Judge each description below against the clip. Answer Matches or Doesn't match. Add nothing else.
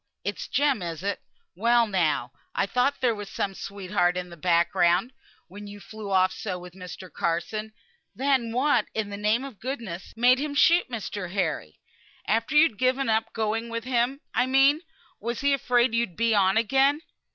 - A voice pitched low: Doesn't match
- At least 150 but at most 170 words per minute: Doesn't match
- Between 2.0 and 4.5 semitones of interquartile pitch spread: Doesn't match